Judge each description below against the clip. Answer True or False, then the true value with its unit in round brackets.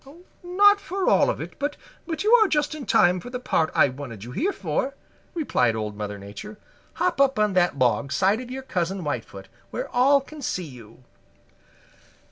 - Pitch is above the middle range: True (210 Hz)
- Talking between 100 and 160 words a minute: False (185 wpm)